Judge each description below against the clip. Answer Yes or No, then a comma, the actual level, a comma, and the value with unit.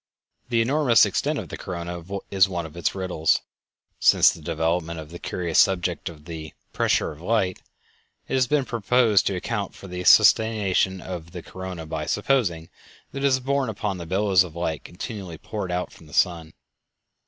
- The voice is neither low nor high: No, very low, 90 Hz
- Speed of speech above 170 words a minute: Yes, average, 180 wpm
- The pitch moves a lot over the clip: No, average, 4.2 semitones